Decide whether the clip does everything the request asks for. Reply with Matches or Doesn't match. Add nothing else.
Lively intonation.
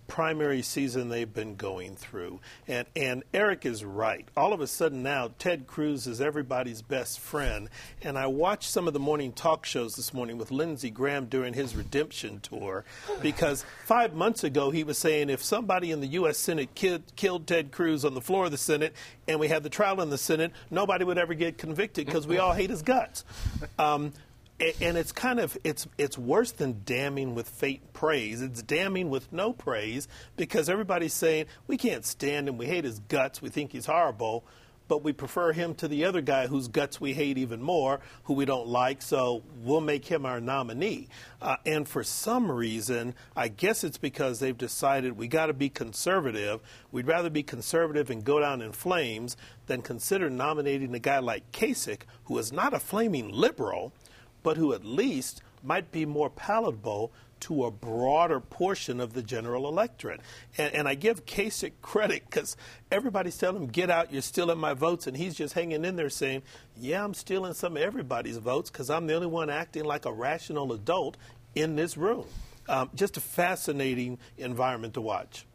Doesn't match